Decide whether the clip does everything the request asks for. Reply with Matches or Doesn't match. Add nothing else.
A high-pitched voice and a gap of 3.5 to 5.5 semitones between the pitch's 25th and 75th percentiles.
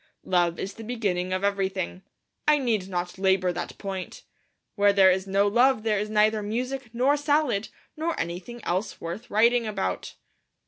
Matches